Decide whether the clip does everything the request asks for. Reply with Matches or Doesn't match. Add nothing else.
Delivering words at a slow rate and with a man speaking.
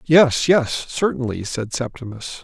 Matches